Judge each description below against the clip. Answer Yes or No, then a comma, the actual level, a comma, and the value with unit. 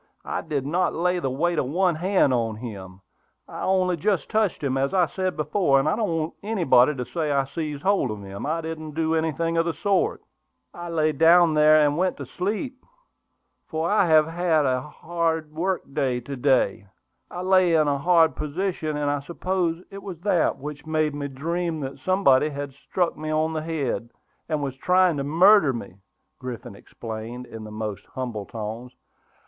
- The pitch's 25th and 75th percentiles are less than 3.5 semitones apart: No, average, 4.3 semitones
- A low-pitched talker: No, medium, 155 Hz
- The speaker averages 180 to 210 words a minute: Yes, average, 190 wpm